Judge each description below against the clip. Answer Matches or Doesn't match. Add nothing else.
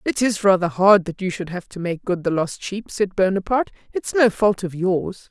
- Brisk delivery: Matches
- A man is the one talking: Doesn't match